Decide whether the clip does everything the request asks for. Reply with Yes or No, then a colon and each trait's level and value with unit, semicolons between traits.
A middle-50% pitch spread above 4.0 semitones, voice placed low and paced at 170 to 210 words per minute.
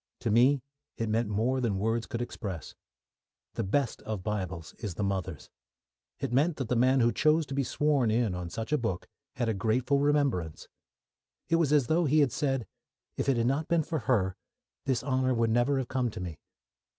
Yes: average, 4.5 semitones; low, 120 Hz; average, 200 wpm